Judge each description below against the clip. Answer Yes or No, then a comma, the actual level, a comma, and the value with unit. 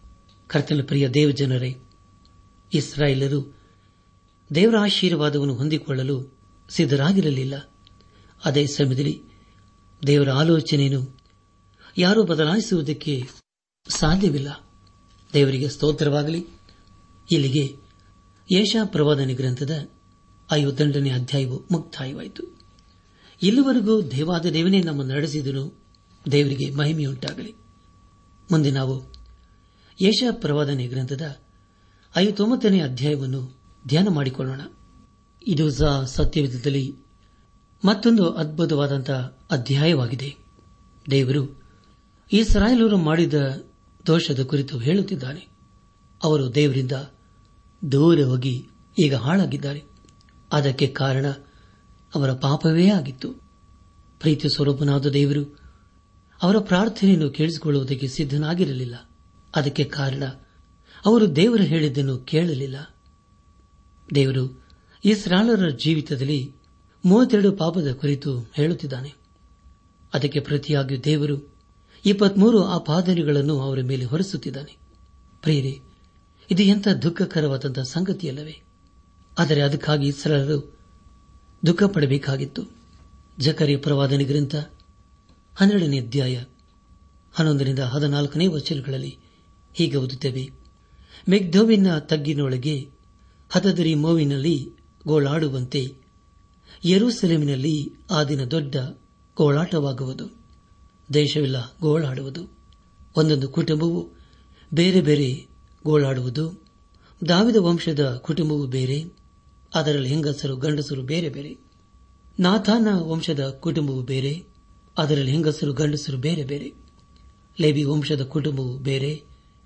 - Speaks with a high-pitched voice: No, medium, 145 Hz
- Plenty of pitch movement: No, average, 3.8 semitones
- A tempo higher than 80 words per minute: No, average, 75 wpm